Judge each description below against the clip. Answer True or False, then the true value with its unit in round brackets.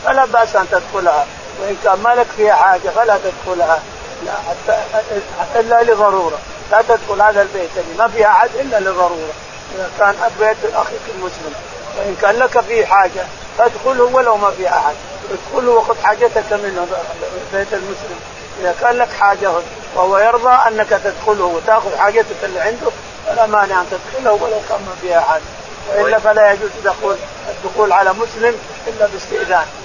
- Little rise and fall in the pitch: False (3.1 semitones)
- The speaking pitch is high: True (210 Hz)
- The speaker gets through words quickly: True (155 wpm)